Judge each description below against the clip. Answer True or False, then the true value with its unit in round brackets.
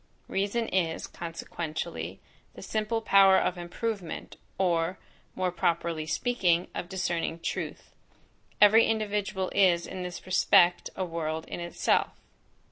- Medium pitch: True (180 Hz)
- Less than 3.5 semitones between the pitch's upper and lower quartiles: True (2.8 semitones)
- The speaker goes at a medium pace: False (120 wpm)